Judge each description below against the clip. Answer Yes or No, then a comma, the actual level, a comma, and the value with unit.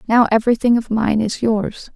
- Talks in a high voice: Yes, high, 225 Hz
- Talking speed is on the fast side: No, average, 185 wpm